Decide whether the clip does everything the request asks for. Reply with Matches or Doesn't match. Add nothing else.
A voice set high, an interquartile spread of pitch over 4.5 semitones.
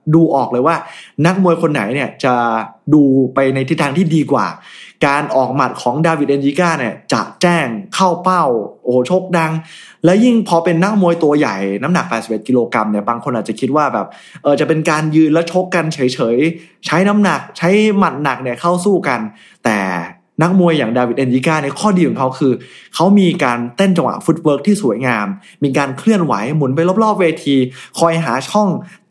Doesn't match